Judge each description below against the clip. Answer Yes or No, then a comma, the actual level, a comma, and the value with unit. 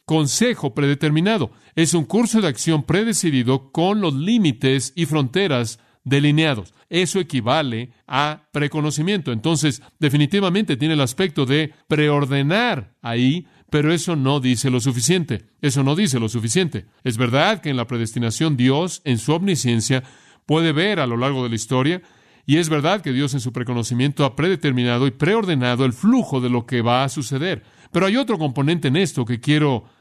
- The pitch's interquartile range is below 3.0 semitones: No, average, 4.5 semitones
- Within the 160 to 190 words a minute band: Yes, average, 165 wpm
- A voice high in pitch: No, medium, 145 Hz